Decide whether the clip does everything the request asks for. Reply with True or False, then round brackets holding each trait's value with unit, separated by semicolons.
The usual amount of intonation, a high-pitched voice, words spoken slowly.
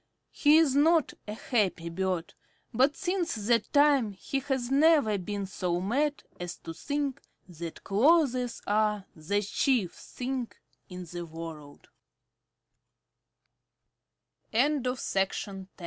False (7.6 semitones; 220 Hz; 105 wpm)